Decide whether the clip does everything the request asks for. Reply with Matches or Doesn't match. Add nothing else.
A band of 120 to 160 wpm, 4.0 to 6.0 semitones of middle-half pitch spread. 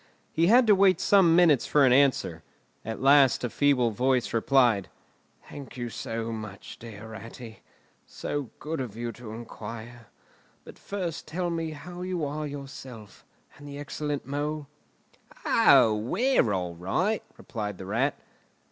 Matches